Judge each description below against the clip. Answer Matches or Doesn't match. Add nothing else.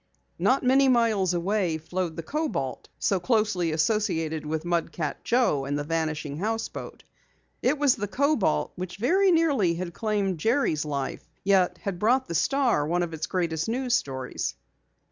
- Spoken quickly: Doesn't match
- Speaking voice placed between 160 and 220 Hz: Matches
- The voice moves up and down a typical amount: Doesn't match